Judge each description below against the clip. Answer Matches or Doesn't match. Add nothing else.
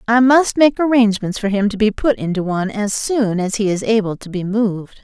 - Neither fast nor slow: Doesn't match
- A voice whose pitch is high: Matches